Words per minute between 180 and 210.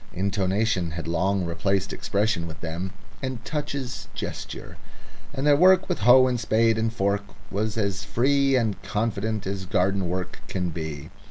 No: average, 155 wpm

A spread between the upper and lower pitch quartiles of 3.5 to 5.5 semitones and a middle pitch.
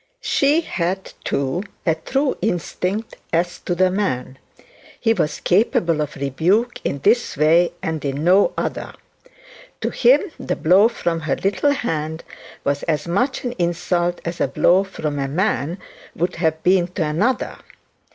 Yes: average, 4.5 semitones; medium, 175 Hz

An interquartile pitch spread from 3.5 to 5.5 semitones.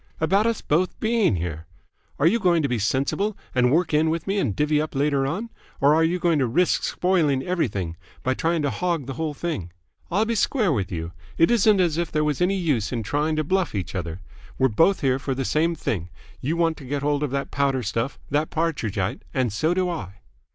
Yes: average, 5.0 semitones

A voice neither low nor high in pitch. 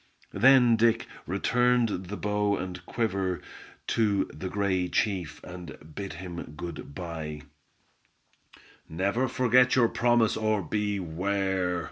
No: low, 100 Hz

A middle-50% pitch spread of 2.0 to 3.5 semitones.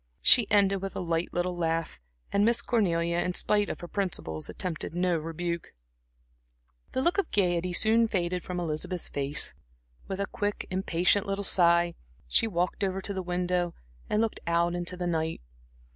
Yes: narrow, 2.6 semitones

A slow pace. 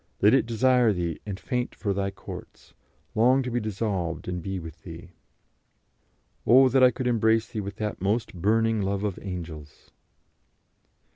No: average, 160 wpm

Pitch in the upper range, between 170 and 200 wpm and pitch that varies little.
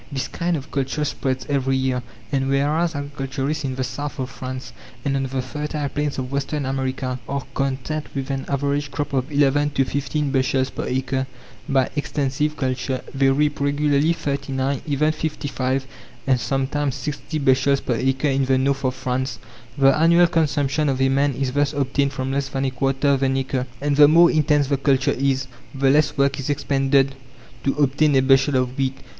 No: low, 135 Hz; average, 185 wpm; narrow, 1.5 semitones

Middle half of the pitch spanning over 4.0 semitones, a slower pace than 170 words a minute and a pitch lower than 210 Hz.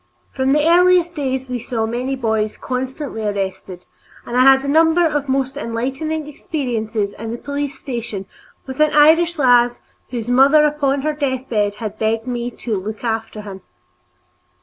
No: average, 4.5 semitones; average, 160 wpm; very high, 255 Hz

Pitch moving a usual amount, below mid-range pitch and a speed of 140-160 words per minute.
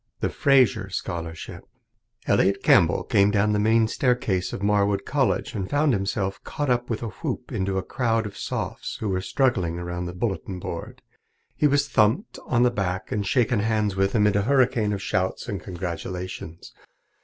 No: average, 3.9 semitones; low, 105 Hz; average, 175 wpm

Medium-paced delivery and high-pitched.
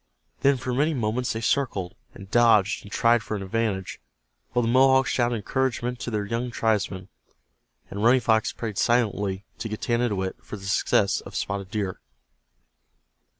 No: average, 155 wpm; low, 115 Hz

